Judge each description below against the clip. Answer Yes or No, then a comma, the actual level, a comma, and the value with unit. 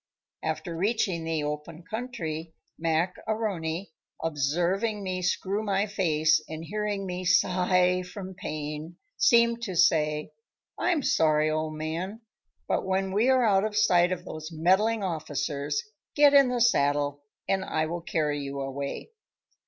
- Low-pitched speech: No, medium, 180 Hz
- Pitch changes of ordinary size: Yes, average, 4.5 semitones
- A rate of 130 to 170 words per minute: Yes, average, 145 wpm